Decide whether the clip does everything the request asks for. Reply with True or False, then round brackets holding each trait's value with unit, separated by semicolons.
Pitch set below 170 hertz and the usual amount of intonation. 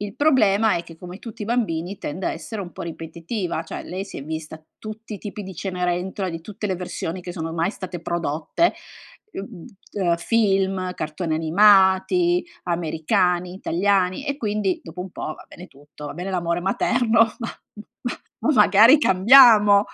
False (190 Hz; 3.7 semitones)